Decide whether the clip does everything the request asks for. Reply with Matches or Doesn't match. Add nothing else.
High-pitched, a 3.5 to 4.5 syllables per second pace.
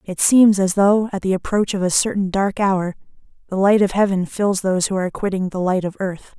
Doesn't match